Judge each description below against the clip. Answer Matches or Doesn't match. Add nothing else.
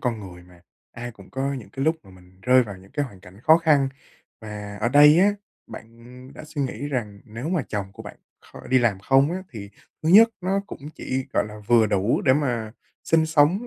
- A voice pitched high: Doesn't match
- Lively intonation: Matches